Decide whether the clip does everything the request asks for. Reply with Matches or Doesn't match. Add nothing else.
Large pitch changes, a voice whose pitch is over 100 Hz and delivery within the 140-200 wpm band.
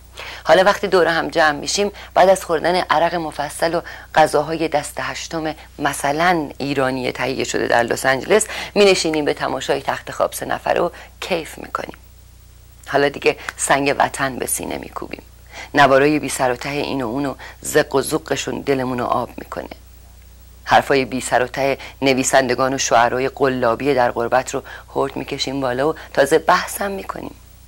Doesn't match